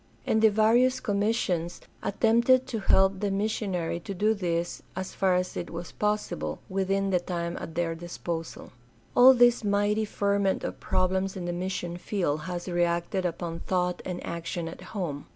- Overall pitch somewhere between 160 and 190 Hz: Yes, medium, 185 Hz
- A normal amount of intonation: Yes, average, 3.2 semitones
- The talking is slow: No, average, 170 wpm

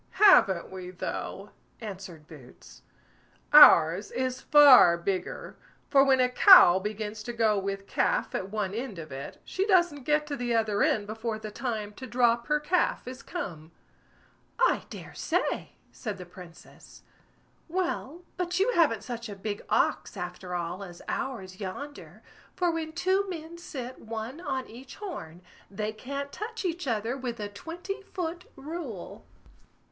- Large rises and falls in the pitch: Yes, wide, 7.4 semitones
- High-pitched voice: Yes, high, 235 Hz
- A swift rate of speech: No, average, 155 wpm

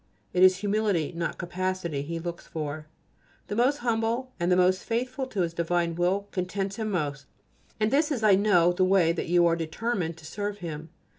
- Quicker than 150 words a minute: Yes, average, 200 wpm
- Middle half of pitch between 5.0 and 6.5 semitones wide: No, average, 4.1 semitones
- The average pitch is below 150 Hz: No, medium, 185 Hz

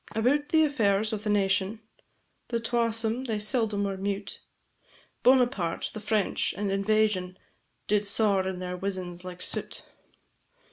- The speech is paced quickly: No, slow, 135 wpm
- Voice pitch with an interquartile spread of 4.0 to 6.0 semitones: No, average, 2.7 semitones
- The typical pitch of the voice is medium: No, high, 210 Hz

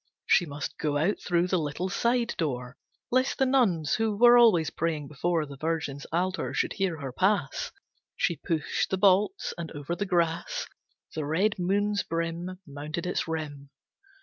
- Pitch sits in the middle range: Yes, medium, 170 Hz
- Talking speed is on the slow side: No, average, 165 wpm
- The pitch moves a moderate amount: Yes, average, 4.7 semitones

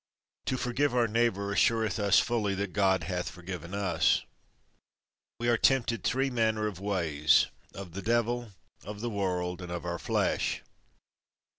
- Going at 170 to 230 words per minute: No, average, 145 wpm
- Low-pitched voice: Yes, low, 100 Hz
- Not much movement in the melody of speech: No, average, 4.4 semitones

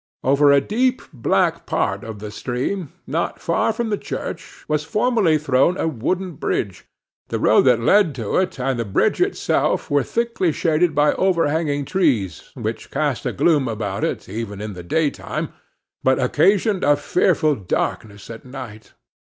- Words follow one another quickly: No, average, 160 wpm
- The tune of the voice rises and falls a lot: Yes, wide, 7.1 semitones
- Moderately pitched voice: Yes, medium, 145 Hz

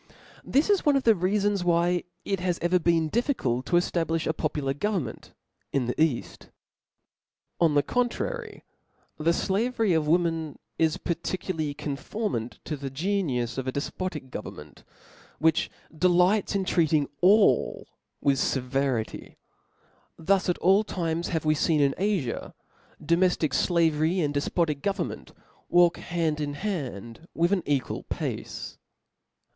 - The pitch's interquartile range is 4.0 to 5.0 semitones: Yes, average, 4.5 semitones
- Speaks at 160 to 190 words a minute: No, average, 140 wpm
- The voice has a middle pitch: Yes, medium, 165 Hz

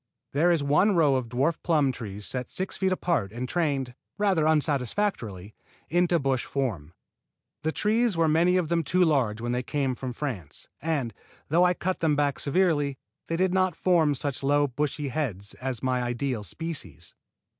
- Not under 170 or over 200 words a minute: Yes, average, 175 wpm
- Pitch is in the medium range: Yes, medium, 145 Hz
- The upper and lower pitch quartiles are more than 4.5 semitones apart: Yes, average, 5.1 semitones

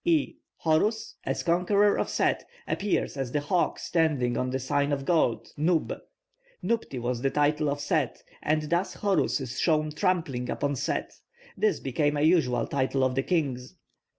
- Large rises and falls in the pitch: No, average, 4.6 semitones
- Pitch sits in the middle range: Yes, medium, 150 Hz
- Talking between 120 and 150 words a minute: No, average, 165 wpm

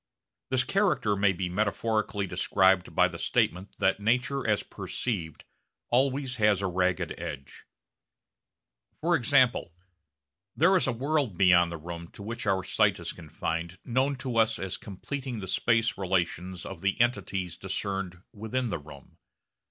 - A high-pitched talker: No, low, 100 Hz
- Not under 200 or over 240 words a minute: No, average, 145 wpm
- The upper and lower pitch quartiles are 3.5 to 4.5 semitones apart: No, average, 5.3 semitones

